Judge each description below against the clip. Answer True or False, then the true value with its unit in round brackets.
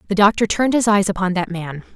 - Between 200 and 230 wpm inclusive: False (245 wpm)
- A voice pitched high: True (195 Hz)